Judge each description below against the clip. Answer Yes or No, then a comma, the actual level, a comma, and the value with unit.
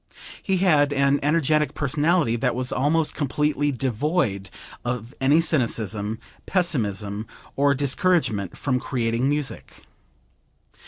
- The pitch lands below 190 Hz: Yes, medium, 140 Hz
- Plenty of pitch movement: No, average, 4.6 semitones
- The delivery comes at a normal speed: No, slow, 105 wpm